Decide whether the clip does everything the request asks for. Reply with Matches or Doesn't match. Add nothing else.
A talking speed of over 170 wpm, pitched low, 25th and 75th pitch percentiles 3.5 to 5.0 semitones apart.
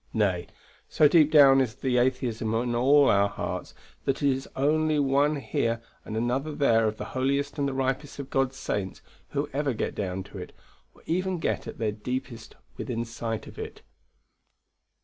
Matches